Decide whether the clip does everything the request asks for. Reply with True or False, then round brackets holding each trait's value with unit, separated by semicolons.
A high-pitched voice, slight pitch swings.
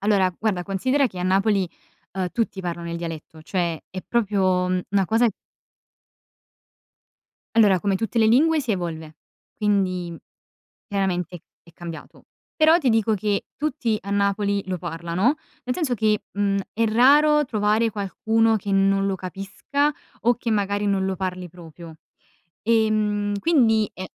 False (200 Hz; 3.4 semitones)